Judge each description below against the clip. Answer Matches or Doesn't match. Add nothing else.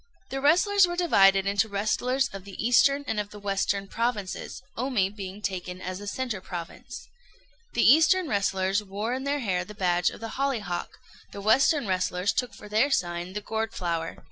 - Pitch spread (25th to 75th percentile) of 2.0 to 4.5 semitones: Doesn't match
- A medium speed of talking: Matches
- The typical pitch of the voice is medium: Doesn't match